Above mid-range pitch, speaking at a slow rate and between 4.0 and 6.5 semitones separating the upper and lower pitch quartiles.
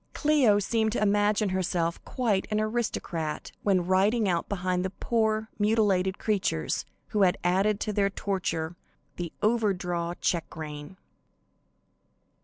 No: high, 195 Hz; slow, 130 wpm; average, 3.2 semitones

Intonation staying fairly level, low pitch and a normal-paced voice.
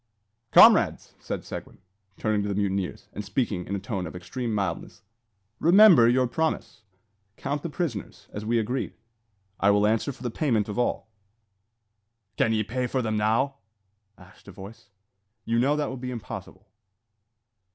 No: average, 4.0 semitones; low, 115 Hz; average, 160 wpm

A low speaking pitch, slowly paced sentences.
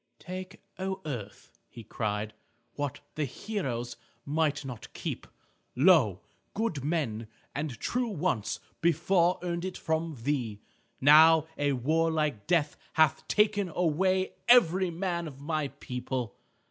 No: medium, 155 Hz; slow, 120 wpm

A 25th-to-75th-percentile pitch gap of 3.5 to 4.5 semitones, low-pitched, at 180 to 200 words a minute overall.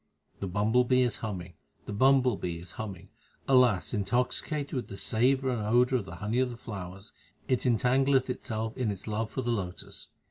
Yes: average, 4.0 semitones; low, 115 Hz; average, 190 wpm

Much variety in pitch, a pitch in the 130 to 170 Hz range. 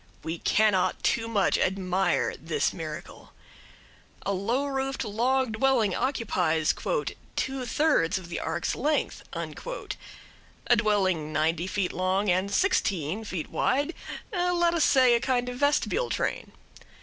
No: wide, 6.3 semitones; high, 220 Hz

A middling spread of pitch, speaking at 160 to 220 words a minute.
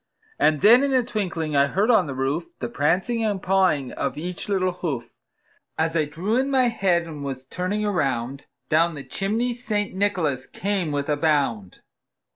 No: wide, 6.3 semitones; average, 180 wpm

